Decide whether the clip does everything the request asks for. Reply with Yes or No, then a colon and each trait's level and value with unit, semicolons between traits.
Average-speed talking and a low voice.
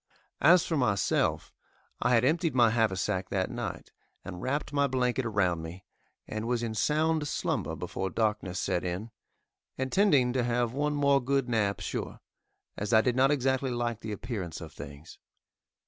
Yes: average, 165 wpm; low, 120 Hz